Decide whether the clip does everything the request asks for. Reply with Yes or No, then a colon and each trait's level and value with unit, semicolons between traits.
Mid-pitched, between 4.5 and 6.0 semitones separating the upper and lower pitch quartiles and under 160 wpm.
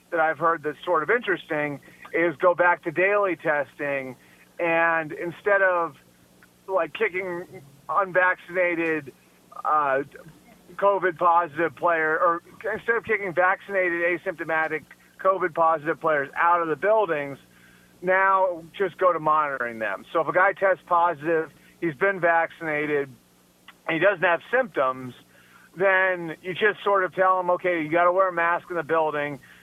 No: medium, 170 Hz; average, 3.2 semitones; average, 150 wpm